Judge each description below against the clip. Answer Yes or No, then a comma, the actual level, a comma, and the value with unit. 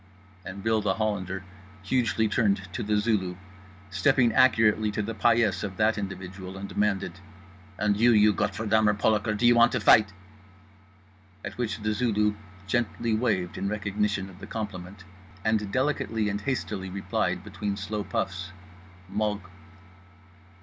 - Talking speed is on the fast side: No, average, 145 wpm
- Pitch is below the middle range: Yes, low, 105 Hz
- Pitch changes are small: Yes, narrow, 2.0 semitones